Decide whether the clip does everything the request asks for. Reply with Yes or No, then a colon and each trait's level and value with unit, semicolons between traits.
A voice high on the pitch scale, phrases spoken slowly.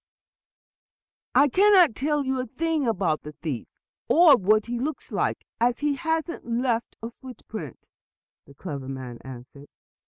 No: high, 240 Hz; average, 150 wpm